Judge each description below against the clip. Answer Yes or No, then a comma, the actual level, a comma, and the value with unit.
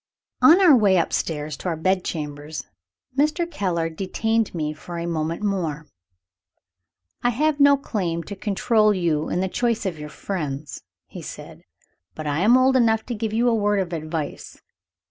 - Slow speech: No, average, 170 wpm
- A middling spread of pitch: No, wide, 6.0 semitones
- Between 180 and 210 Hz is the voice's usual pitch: Yes, high, 190 Hz